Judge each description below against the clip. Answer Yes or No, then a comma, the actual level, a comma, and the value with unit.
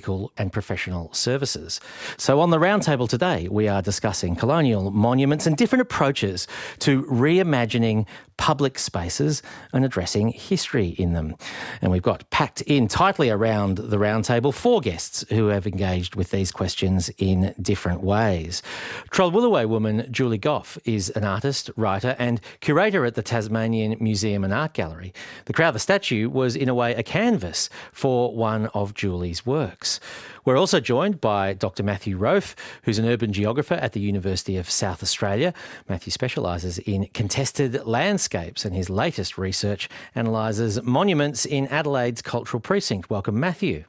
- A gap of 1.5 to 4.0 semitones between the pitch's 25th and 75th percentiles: No, wide, 5.6 semitones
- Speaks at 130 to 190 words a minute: Yes, average, 150 wpm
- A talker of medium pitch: No, low, 110 Hz